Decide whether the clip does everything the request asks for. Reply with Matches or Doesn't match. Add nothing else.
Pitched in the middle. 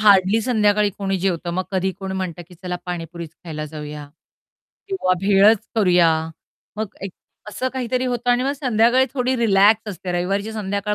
Doesn't match